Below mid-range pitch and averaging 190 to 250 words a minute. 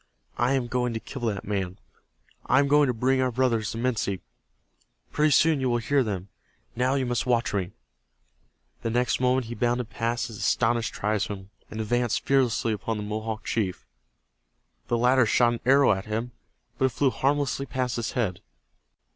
No: low, 120 Hz; average, 180 wpm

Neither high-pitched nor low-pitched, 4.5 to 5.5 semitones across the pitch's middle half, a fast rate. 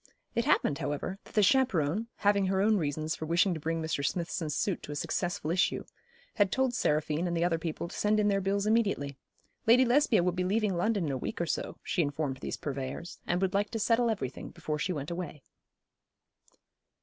Yes: medium, 180 Hz; average, 5.0 semitones; fast, 210 wpm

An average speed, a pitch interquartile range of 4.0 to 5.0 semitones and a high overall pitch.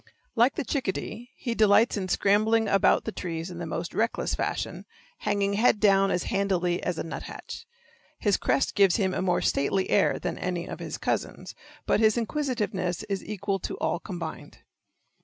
No: average, 175 wpm; average, 3.4 semitones; high, 195 Hz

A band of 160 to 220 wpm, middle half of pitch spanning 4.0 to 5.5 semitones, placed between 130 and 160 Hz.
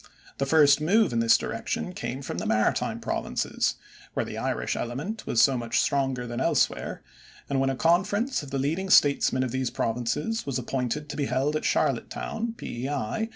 Yes: average, 180 wpm; average, 4.6 semitones; medium, 140 Hz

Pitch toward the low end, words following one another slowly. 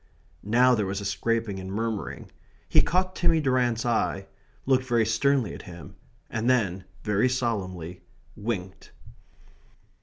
Yes: low, 115 Hz; slow, 130 wpm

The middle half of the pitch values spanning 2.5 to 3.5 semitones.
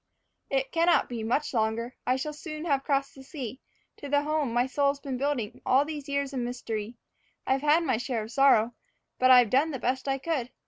Yes: average, 2.9 semitones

